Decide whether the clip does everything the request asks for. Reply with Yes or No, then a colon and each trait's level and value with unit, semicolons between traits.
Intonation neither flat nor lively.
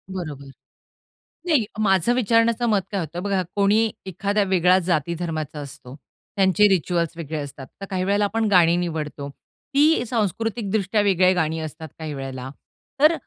Yes: average, 4.8 semitones